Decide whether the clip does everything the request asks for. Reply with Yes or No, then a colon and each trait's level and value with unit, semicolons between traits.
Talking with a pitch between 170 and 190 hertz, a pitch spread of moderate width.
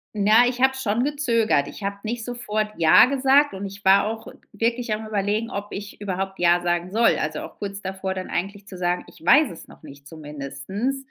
No: high, 205 Hz; average, 4.1 semitones